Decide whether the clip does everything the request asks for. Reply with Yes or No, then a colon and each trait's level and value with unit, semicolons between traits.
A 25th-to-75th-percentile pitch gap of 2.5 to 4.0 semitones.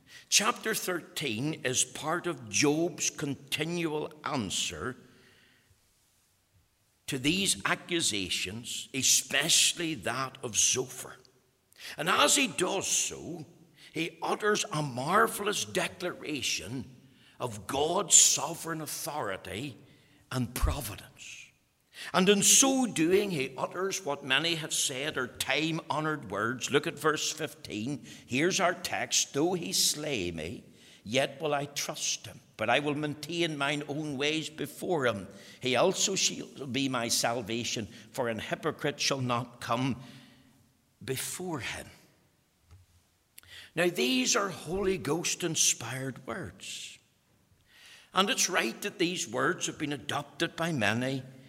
No: average, 4.9 semitones